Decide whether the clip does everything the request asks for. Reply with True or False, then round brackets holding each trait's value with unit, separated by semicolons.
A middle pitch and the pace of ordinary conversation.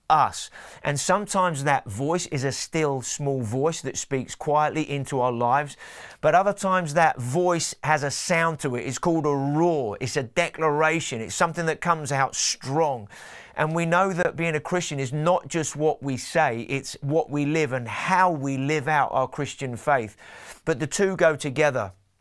True (150 Hz; 185 wpm)